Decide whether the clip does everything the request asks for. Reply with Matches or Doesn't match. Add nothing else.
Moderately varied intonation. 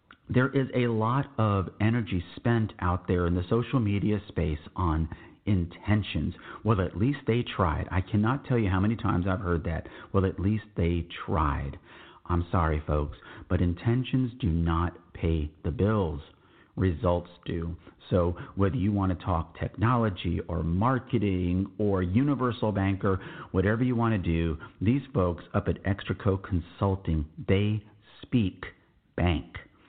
Matches